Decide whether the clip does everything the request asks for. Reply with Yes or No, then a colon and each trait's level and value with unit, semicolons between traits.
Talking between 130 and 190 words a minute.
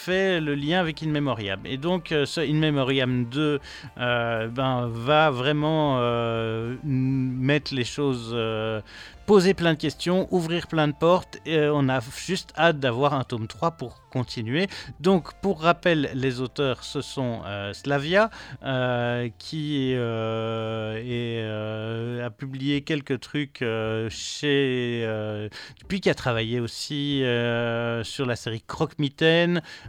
Yes: slow, 145 wpm